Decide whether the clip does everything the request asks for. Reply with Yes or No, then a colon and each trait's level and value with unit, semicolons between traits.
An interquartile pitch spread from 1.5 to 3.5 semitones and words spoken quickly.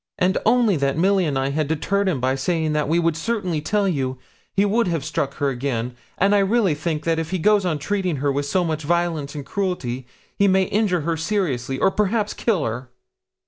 No: wide, 5.5 semitones; fast, 210 wpm